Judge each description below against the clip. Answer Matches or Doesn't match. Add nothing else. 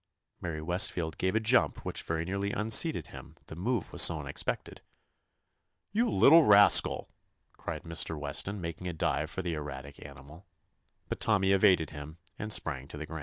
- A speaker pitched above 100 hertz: Doesn't match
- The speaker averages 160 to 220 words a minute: Matches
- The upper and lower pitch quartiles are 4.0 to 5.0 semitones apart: Matches